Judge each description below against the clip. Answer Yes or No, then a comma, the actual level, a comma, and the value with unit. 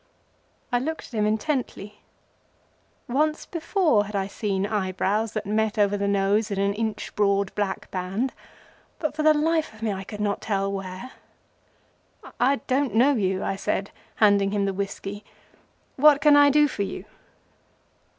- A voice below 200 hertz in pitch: No, high, 210 Hz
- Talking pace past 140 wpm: Yes, average, 160 wpm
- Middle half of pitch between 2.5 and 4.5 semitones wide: No, average, 4.9 semitones